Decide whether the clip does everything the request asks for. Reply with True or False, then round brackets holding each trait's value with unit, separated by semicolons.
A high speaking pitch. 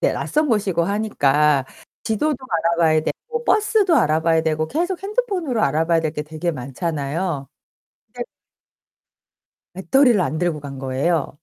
False (170 Hz)